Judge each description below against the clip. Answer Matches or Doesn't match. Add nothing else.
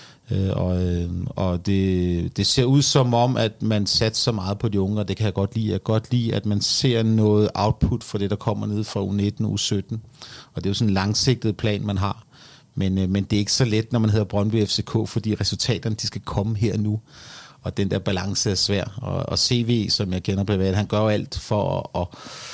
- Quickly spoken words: Matches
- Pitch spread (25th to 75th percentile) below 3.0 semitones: Matches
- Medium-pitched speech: Doesn't match